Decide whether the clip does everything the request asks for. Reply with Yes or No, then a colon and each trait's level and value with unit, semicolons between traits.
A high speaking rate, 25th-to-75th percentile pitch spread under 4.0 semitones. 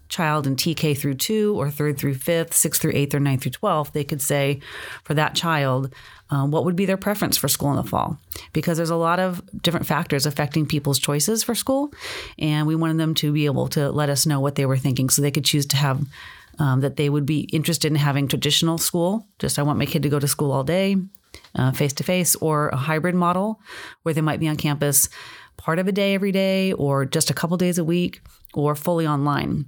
Yes: fast, 235 wpm; average, 3.2 semitones